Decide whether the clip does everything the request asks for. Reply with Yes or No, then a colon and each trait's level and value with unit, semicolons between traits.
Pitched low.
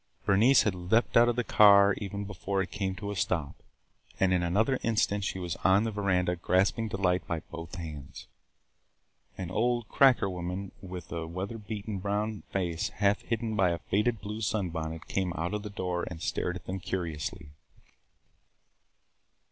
Yes: very low, 95 Hz